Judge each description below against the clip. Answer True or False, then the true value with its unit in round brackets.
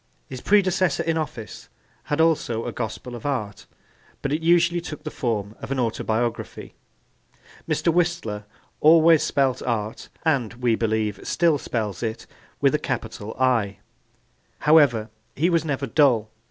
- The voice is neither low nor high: False (130 Hz)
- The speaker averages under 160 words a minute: True (140 wpm)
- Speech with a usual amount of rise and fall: False (6.4 semitones)